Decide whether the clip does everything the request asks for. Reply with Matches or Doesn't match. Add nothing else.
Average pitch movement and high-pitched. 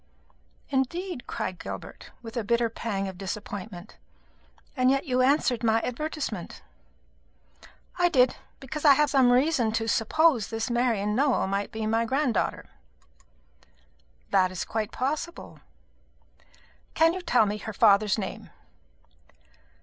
Matches